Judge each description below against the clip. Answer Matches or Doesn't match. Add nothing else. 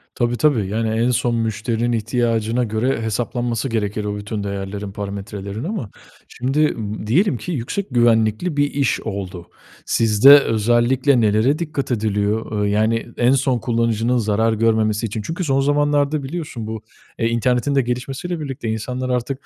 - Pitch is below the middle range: Matches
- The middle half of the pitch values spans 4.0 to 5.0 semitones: Doesn't match